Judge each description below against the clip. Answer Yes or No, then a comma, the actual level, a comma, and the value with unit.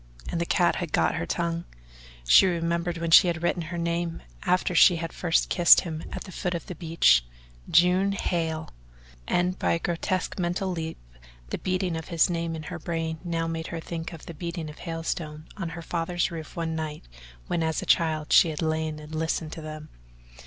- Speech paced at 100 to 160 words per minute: No, average, 200 wpm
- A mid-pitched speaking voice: Yes, medium, 165 Hz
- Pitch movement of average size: No, narrow, 1.4 semitones